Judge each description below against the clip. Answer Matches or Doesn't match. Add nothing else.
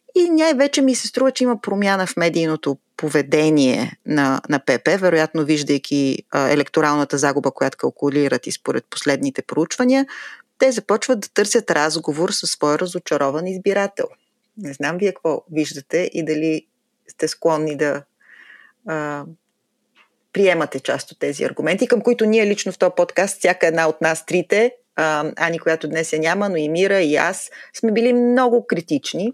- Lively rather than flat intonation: Matches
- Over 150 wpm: Matches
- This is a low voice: Doesn't match